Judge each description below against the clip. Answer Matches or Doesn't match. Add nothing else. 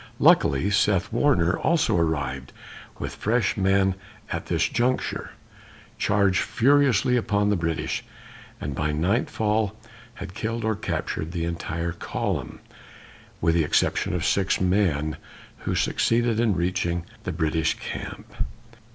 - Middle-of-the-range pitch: Doesn't match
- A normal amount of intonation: Matches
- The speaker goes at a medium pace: Doesn't match